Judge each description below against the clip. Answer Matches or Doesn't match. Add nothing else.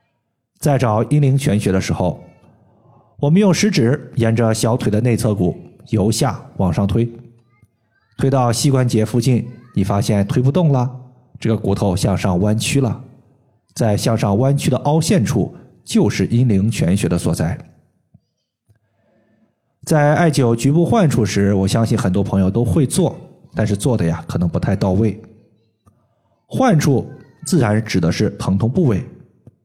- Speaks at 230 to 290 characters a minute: Doesn't match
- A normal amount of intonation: Matches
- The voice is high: Doesn't match